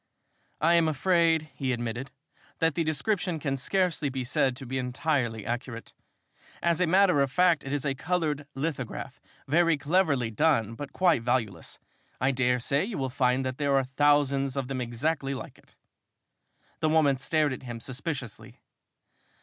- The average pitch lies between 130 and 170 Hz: Yes, medium, 140 Hz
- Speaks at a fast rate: No, average, 165 wpm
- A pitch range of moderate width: Yes, average, 4.0 semitones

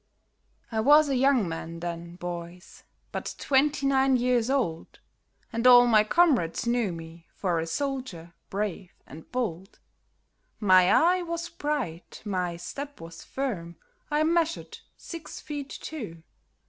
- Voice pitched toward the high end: Yes, high, 230 Hz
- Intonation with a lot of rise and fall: Yes, wide, 8.4 semitones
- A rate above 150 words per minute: No, slow, 135 wpm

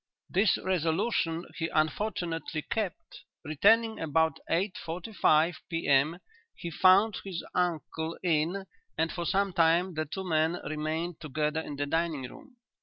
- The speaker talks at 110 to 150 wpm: Yes, slow, 135 wpm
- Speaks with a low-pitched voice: No, medium, 165 Hz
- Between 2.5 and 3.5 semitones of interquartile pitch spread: Yes, average, 2.9 semitones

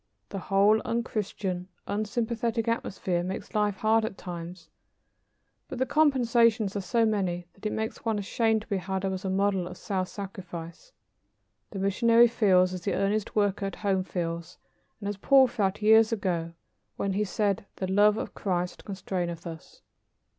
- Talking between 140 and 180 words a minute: Yes, average, 165 wpm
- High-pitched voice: Yes, high, 200 Hz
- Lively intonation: No, average, 3.0 semitones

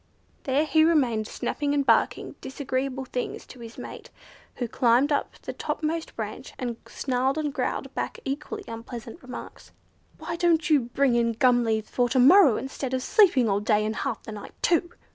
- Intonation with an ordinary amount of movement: Yes, average, 3.9 semitones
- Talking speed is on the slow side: No, average, 180 wpm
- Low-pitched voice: No, very high, 260 Hz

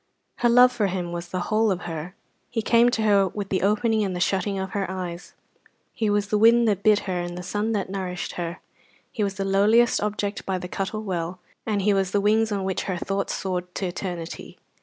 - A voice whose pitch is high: Yes, high, 195 Hz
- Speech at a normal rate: No, fast, 225 wpm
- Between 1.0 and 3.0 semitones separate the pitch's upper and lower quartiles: Yes, average, 2.7 semitones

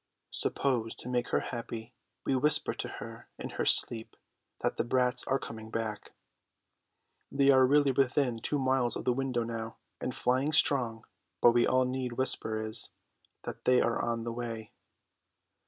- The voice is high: No, low, 125 Hz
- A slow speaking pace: No, average, 165 wpm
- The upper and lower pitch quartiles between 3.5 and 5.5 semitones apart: No, narrow, 2.4 semitones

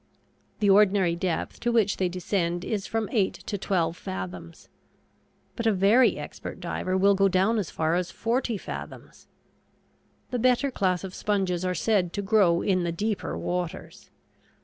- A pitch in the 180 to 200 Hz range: Yes, high, 190 Hz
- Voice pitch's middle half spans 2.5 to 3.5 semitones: Yes, average, 3.2 semitones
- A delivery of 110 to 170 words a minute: Yes, average, 160 wpm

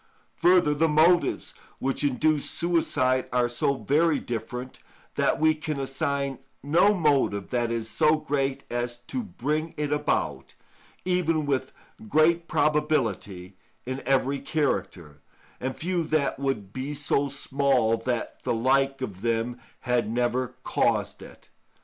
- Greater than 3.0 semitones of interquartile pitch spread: Yes, average, 4.0 semitones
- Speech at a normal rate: No, slow, 130 wpm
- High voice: No, low, 135 Hz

